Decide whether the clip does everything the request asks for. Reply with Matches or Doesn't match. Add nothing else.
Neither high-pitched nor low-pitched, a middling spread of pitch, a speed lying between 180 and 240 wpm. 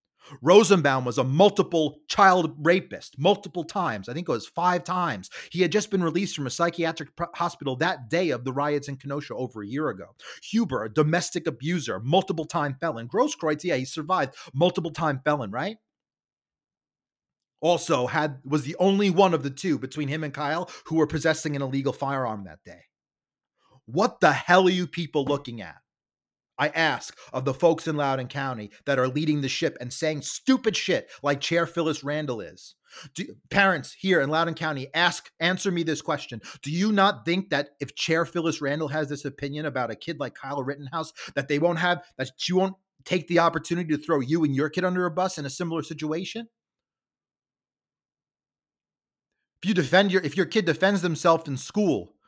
Matches